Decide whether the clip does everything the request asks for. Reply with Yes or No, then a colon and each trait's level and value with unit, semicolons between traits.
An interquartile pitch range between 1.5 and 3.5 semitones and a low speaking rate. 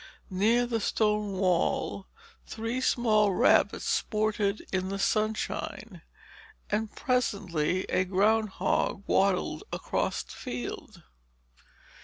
Yes: average, 2.7 semitones; slow, 95 wpm